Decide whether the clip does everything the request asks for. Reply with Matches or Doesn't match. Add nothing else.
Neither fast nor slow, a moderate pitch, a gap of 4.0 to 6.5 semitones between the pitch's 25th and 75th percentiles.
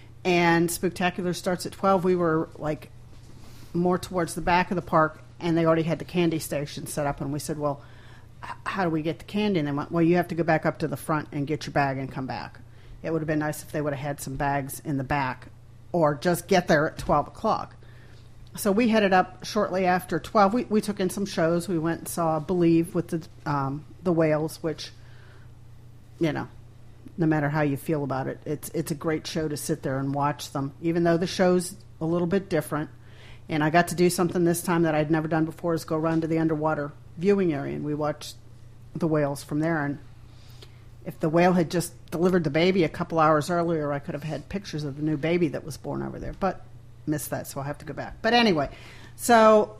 Doesn't match